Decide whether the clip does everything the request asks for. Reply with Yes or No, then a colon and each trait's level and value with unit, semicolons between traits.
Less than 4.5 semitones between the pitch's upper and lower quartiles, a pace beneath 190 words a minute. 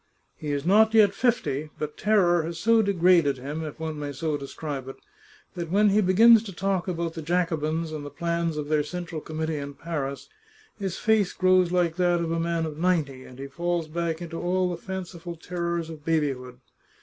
No: average, 3.0 semitones; average, 195 wpm